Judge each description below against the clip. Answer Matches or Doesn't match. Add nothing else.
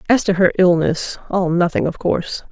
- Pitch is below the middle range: Doesn't match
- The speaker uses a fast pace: Doesn't match